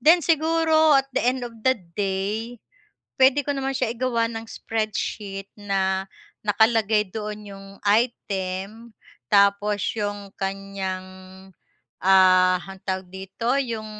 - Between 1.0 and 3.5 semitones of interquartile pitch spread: No, average, 3.9 semitones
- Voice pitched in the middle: No, high, 210 Hz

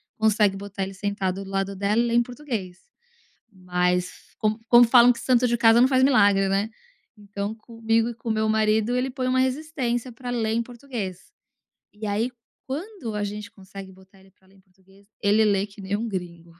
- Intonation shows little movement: No, average, 3.5 semitones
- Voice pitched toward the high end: Yes, high, 215 Hz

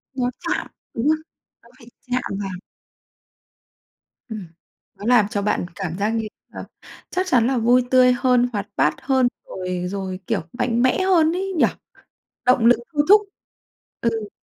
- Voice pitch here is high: Yes, high, 240 Hz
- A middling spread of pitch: Yes, average, 4.0 semitones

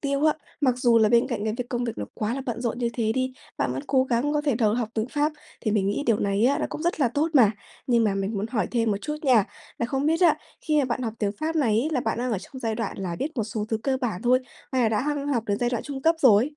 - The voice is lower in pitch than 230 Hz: No, high, 240 Hz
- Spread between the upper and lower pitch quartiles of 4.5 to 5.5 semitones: No, average, 4.0 semitones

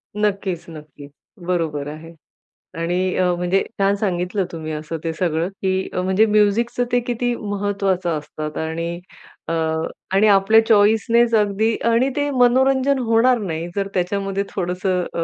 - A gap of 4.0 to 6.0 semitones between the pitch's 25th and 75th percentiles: Yes, average, 4.4 semitones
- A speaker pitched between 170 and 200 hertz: Yes, high, 195 Hz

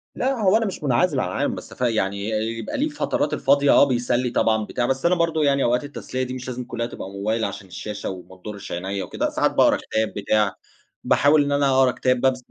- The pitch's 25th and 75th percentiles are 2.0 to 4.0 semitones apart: No, average, 4.8 semitones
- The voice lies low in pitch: Yes, low, 125 Hz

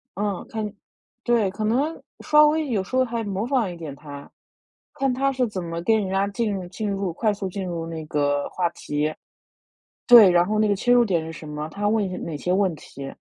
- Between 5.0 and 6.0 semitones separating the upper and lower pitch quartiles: Yes, average, 5.3 semitones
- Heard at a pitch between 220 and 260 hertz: No, high, 195 Hz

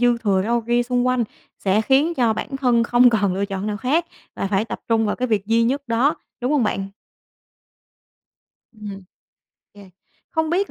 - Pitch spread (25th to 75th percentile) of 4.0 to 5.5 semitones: No, average, 3.4 semitones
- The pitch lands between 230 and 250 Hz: Yes, high, 235 Hz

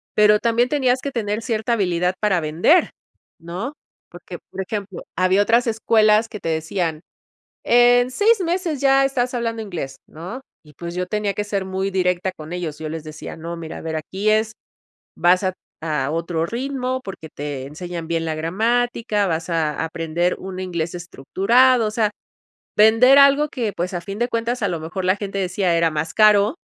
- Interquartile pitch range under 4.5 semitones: No, wide, 5.6 semitones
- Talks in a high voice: Yes, high, 195 Hz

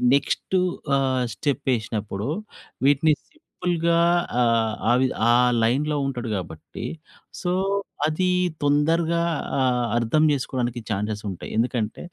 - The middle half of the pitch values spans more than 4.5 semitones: Yes, average, 5.2 semitones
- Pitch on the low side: Yes, low, 130 Hz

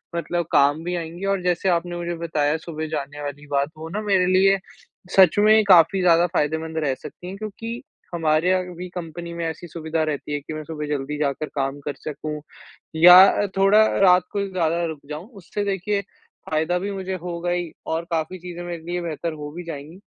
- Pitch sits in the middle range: Yes, medium, 170 Hz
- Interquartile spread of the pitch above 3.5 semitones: No, average, 2.8 semitones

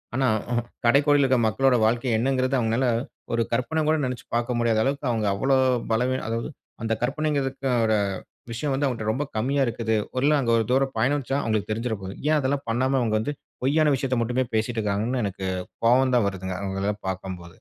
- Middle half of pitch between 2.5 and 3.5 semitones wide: Yes, average, 3.2 semitones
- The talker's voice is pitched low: Yes, low, 120 Hz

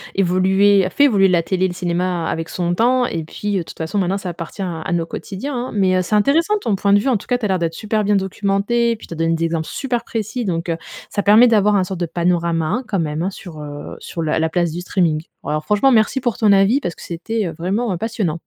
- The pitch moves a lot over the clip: No, average, 4.0 semitones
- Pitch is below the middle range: No, high, 190 Hz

